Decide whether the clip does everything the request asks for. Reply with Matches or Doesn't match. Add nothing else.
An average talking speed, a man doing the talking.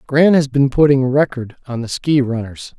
Matches